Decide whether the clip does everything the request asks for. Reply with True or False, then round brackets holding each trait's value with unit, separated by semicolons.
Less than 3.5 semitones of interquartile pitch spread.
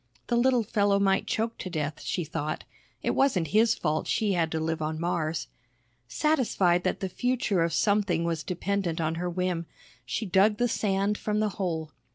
False (4.3 semitones)